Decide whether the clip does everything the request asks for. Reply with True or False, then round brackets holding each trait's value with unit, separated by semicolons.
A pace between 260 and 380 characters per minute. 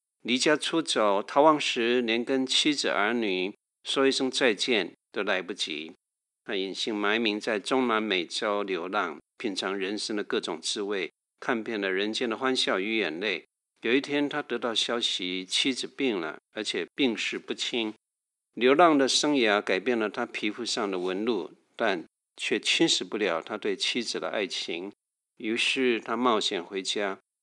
False (235 characters per minute)